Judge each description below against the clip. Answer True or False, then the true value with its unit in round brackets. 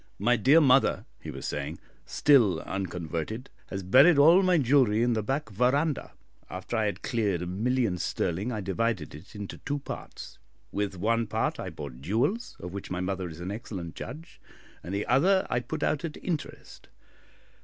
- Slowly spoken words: False (175 wpm)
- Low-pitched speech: True (110 Hz)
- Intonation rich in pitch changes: True (6.5 semitones)